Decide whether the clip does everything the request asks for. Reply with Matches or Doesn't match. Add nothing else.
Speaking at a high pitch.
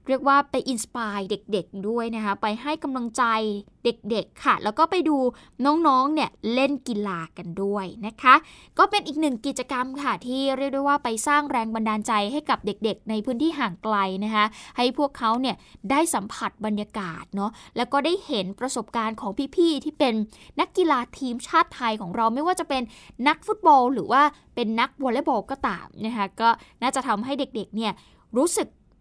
Matches